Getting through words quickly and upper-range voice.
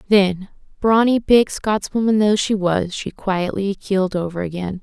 No: average, 150 wpm; high, 200 Hz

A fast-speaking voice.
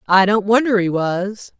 No: average, 190 wpm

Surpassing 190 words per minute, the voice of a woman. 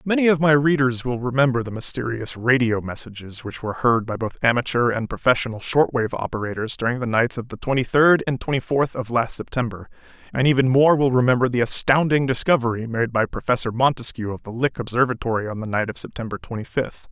No: average, 200 wpm; male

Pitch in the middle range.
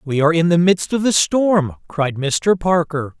Yes: medium, 170 Hz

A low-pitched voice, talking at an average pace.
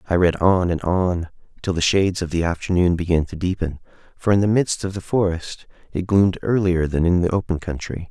No: very low, 90 Hz; fast, 215 wpm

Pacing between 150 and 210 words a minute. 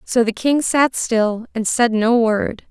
Yes: average, 200 wpm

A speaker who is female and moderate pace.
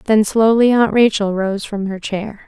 Yes: female; average, 195 wpm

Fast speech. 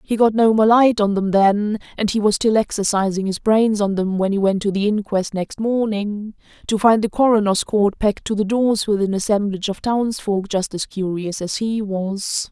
Yes: fast, 210 wpm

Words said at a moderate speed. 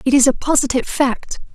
Yes: average, 195 wpm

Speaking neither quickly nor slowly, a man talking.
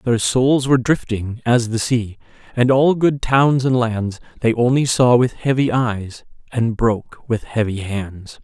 Yes: average, 170 wpm; male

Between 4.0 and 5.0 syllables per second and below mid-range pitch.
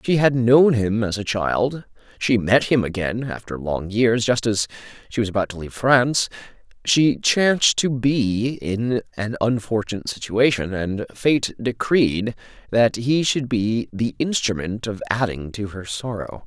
Yes: 4.3 syllables/s; low, 115 Hz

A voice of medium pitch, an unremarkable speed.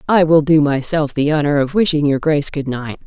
No: medium, 150 Hz; fast, 235 wpm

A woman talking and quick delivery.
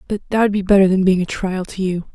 Yes: female; fast, 310 wpm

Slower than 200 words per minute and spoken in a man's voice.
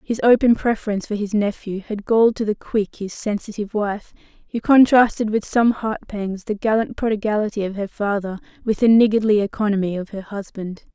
No: average, 180 wpm; female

